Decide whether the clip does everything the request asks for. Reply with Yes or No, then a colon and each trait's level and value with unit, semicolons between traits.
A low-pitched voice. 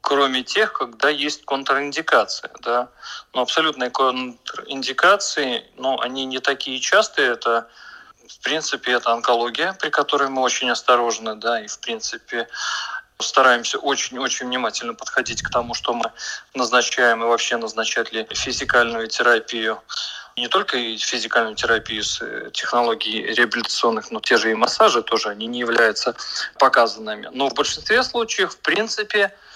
Yes: low, 130 Hz